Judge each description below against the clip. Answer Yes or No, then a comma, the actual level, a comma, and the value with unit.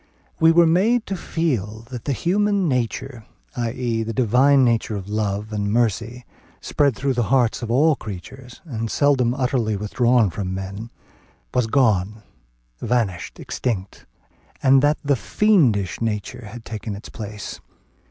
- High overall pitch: No, low, 120 Hz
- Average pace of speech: Yes, average, 150 wpm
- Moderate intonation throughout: Yes, average, 4.3 semitones